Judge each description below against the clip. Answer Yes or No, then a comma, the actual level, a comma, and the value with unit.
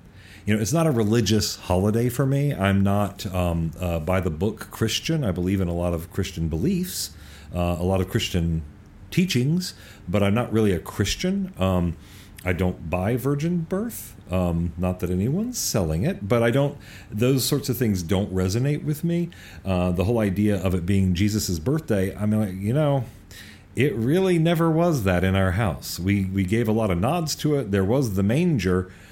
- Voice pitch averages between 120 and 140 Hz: No, low, 100 Hz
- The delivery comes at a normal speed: Yes, average, 190 wpm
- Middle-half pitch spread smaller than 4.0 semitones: No, wide, 5.6 semitones